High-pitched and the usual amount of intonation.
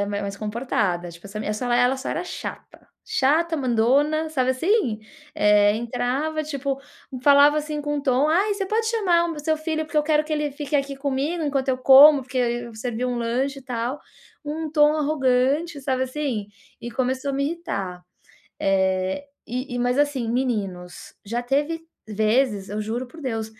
Yes: very high, 265 Hz; average, 4.1 semitones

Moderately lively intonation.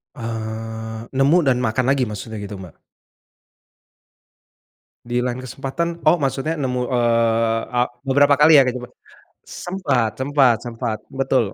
Yes: average, 3.3 semitones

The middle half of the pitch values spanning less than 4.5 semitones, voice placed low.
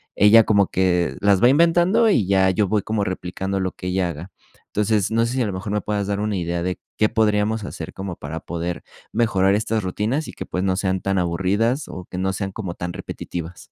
Yes: average, 2.8 semitones; very low, 95 Hz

